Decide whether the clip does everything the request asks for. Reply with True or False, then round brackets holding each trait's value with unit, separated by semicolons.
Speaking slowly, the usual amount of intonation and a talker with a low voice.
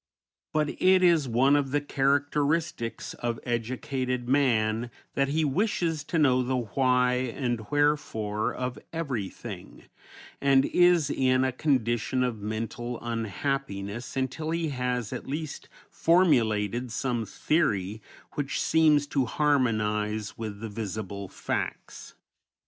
True (120 wpm; 4.4 semitones; 130 Hz)